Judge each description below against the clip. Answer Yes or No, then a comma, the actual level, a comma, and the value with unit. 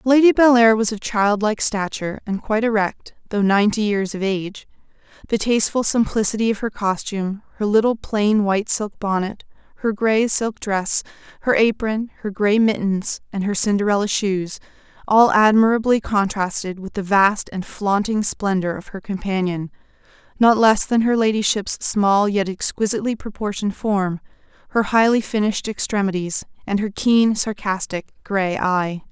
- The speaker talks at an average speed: Yes, average, 145 wpm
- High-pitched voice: Yes, high, 205 Hz